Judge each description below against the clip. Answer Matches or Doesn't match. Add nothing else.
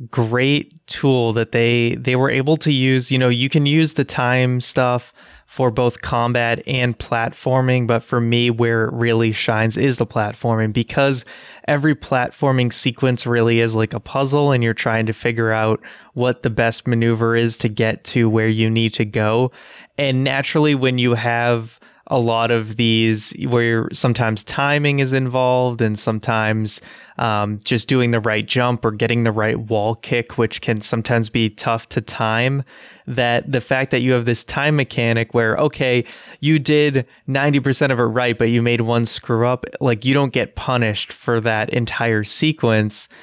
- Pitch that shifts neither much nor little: Doesn't match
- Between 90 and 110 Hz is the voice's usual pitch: Doesn't match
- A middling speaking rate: Matches